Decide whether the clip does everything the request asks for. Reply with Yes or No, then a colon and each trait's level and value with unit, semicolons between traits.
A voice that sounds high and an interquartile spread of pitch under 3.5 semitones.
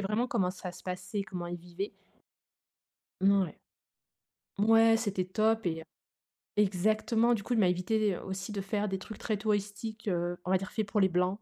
Yes: high, 200 Hz; average, 2.9 semitones